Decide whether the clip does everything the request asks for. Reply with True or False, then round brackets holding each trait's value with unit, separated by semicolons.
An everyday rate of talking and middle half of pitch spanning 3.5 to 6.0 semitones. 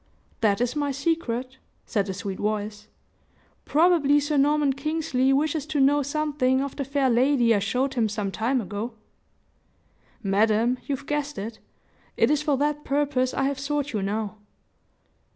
True (155 wpm; 4.7 semitones)